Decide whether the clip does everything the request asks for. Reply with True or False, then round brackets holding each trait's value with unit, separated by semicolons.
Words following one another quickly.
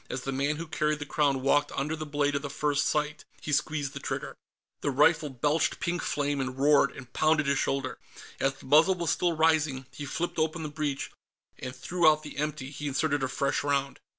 True (215 wpm)